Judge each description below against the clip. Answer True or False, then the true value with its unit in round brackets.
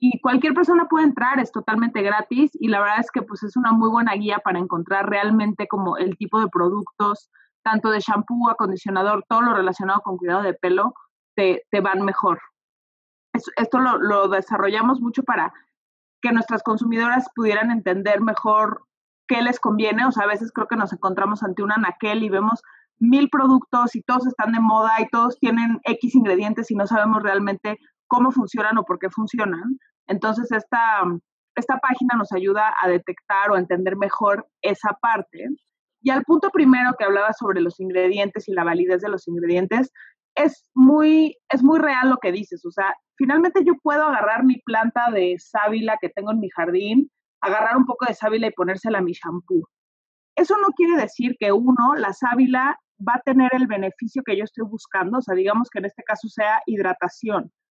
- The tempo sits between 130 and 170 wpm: False (185 wpm)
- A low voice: False (220 Hz)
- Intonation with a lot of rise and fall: False (4.0 semitones)